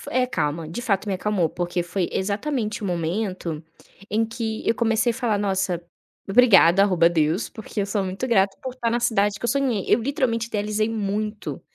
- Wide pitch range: No, average, 3.6 semitones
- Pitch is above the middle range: Yes, high, 205 Hz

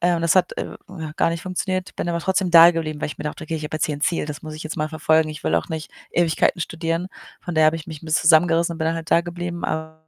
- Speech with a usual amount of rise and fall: No, narrow, 1.5 semitones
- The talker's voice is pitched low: No, medium, 165 Hz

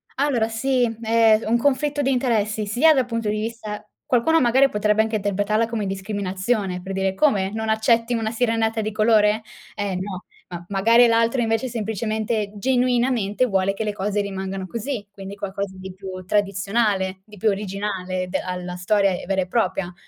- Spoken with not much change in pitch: No, average, 3.0 semitones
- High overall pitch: Yes, high, 215 Hz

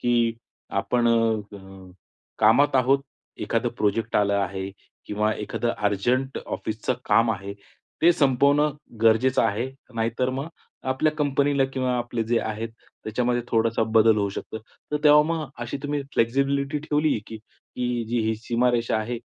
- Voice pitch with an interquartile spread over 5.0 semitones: No, average, 3.4 semitones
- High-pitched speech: No, low, 120 Hz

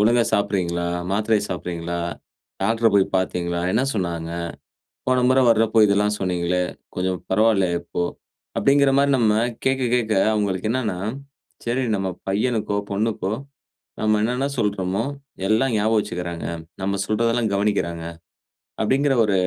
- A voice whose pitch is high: No, low, 105 Hz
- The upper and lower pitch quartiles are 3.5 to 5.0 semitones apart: Yes, average, 3.8 semitones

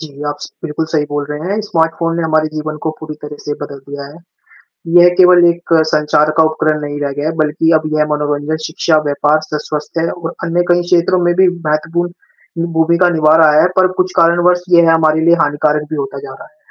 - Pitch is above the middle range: No, medium, 155 Hz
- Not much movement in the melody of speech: Yes, narrow, 2.2 semitones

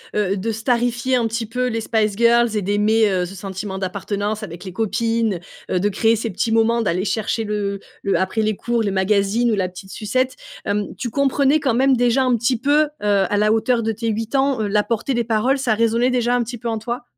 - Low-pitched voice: No, high, 225 Hz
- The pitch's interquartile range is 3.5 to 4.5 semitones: No, average, 2.7 semitones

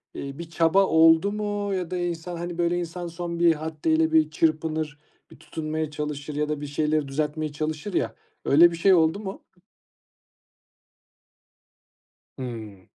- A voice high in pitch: No, medium, 160 Hz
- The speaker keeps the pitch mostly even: Yes, narrow, 2.3 semitones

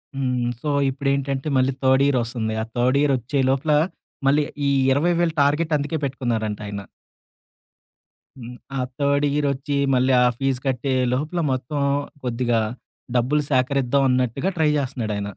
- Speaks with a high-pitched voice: No, low, 135 Hz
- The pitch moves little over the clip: Yes, narrow, 2.3 semitones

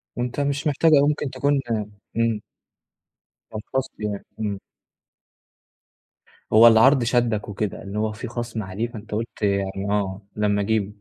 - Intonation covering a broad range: No, average, 3.2 semitones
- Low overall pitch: Yes, low, 110 Hz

